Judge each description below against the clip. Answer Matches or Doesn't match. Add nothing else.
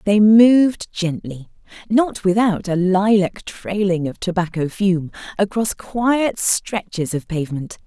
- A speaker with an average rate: Doesn't match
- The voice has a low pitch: Doesn't match